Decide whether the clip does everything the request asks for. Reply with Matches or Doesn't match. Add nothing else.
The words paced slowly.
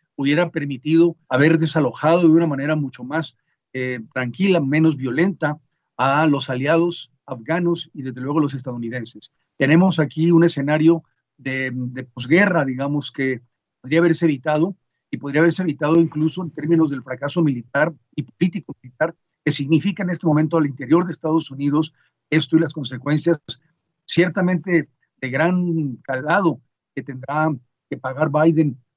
Doesn't match